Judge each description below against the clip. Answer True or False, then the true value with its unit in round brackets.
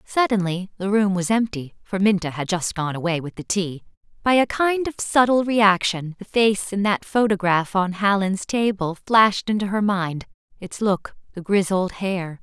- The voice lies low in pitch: False (195 Hz)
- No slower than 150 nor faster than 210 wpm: True (160 wpm)